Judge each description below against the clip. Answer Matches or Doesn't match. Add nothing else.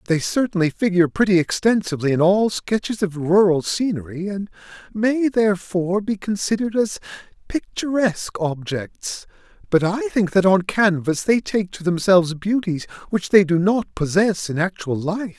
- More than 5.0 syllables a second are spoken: Doesn't match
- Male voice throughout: Matches